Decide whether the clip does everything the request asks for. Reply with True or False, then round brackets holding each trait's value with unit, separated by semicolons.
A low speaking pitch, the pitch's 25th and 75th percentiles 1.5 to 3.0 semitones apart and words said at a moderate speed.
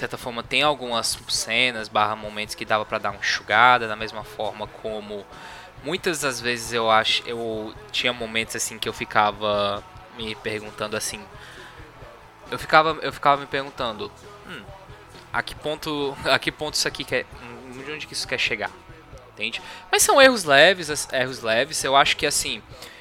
False (115 Hz; 4.2 semitones; 170 wpm)